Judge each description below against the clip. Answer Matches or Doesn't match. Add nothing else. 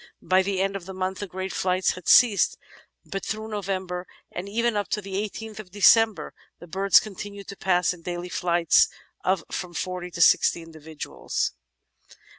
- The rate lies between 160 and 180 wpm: Matches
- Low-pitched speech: Doesn't match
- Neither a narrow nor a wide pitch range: Doesn't match